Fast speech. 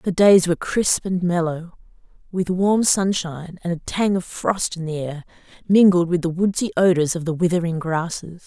No: average, 185 wpm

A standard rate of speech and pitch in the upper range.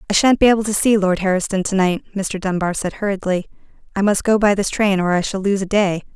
No: fast, 255 wpm; high, 195 Hz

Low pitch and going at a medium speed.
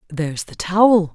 No: medium, 180 Hz; average, 155 wpm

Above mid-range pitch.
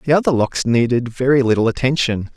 No: low, 125 Hz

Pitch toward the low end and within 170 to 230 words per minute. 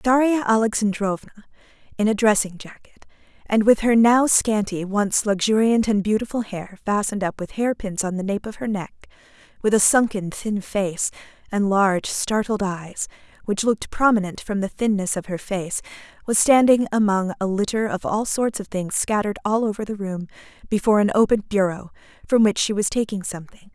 No: high, 210 Hz; average, 175 wpm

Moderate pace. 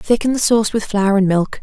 No: fast, 260 wpm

